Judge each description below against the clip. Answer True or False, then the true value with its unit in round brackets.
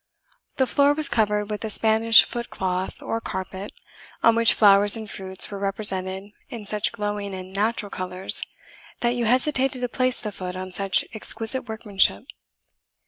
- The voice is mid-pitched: False (210 Hz)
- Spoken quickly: False (160 wpm)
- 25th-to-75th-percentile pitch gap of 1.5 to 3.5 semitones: True (3.1 semitones)